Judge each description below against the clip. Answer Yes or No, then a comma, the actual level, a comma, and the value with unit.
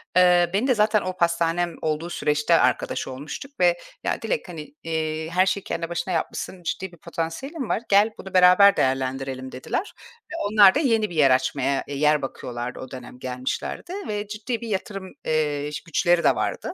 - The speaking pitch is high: No, medium, 170 Hz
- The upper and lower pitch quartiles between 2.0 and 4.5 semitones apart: No, average, 5.3 semitones